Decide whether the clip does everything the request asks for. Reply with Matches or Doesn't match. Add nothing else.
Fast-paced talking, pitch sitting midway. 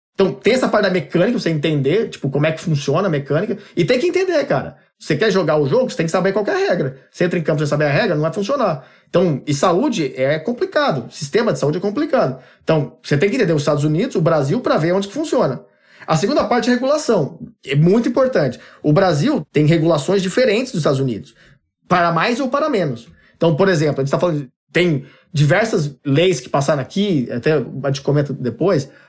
Matches